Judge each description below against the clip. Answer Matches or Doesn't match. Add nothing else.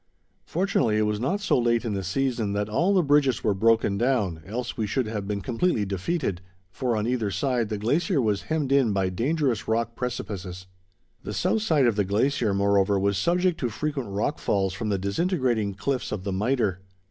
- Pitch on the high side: Doesn't match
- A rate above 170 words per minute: Matches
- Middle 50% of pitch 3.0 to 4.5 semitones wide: Doesn't match